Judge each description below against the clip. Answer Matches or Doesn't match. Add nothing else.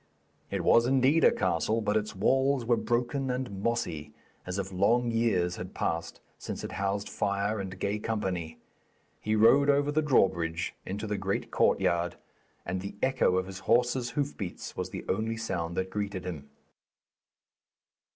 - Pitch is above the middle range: Doesn't match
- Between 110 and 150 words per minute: Doesn't match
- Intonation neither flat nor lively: Matches